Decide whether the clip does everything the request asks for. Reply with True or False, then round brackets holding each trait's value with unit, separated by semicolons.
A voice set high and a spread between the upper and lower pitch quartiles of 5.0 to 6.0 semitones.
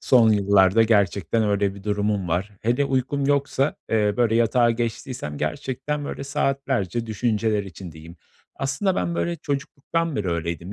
False (115 Hz; 5.4 semitones)